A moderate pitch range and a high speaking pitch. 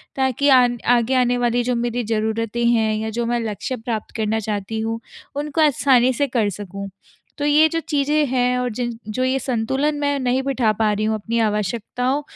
Yes: average, 3.1 semitones; high, 240 Hz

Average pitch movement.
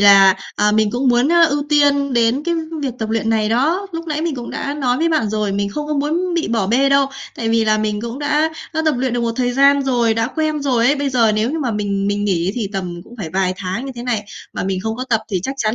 Yes: average, 4.9 semitones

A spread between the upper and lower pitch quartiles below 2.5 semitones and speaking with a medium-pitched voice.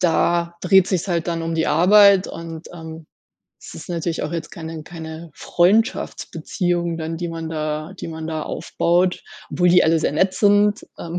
Yes: narrow, 1.8 semitones; medium, 170 Hz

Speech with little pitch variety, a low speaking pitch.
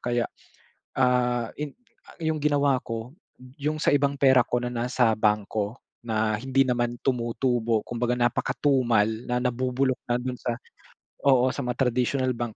Yes: narrow, 2.1 semitones; low, 125 Hz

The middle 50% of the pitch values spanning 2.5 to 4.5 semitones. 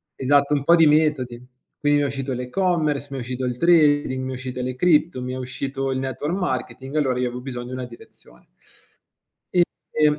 Yes: average, 2.8 semitones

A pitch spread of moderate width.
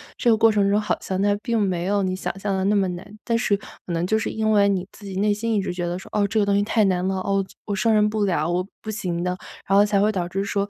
No: narrow, 2.1 semitones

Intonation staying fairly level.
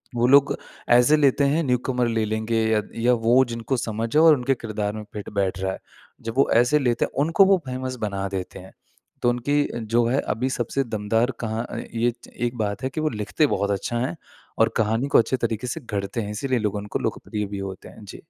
No: average, 3.4 semitones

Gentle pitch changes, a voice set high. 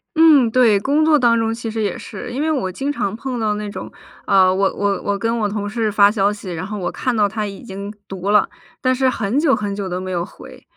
No: average, 3.8 semitones; high, 210 Hz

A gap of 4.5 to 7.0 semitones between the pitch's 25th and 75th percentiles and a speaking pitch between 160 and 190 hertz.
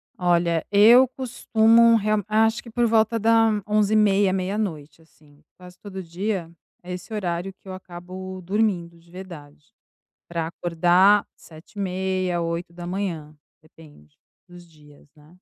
No: average, 3.7 semitones; medium, 185 Hz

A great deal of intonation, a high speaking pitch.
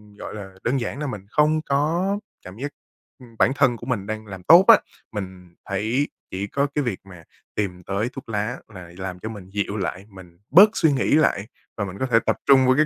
No: wide, 6.2 semitones; low, 110 Hz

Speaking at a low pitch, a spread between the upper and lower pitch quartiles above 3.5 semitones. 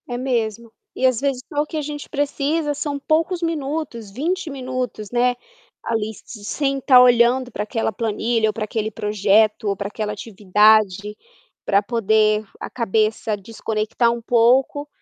No: high, 235 Hz; average, 4.3 semitones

